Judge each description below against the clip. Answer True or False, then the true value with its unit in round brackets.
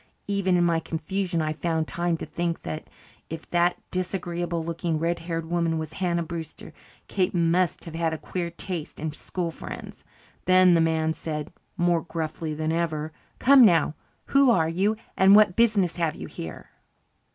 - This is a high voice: False (170 Hz)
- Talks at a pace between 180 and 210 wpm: False (170 wpm)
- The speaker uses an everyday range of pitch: False (2.0 semitones)